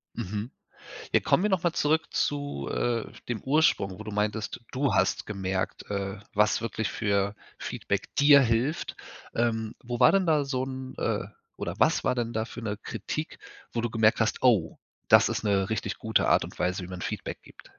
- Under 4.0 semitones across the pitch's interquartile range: No, average, 4.4 semitones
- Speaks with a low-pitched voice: Yes, low, 115 Hz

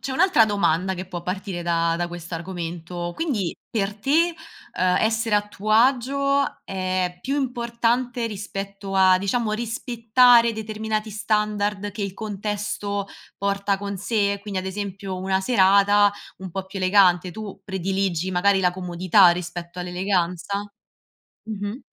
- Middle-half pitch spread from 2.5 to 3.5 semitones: Yes, average, 2.8 semitones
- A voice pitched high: Yes, high, 200 Hz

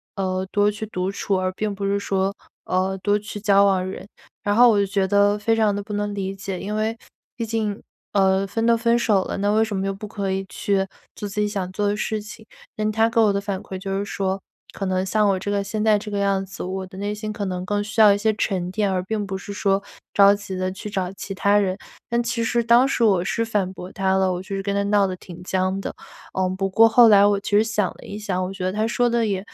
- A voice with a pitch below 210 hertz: Yes, high, 200 Hz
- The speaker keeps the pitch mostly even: Yes, narrow, 1.8 semitones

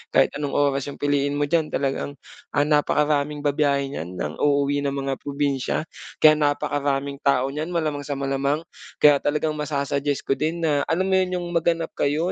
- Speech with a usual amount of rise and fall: No, narrow, 1.5 semitones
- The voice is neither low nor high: Yes, medium, 145 Hz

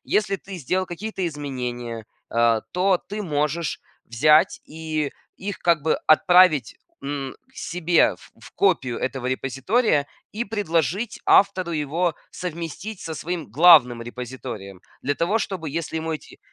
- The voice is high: No, medium, 160 Hz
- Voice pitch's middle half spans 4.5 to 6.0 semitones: Yes, average, 5.2 semitones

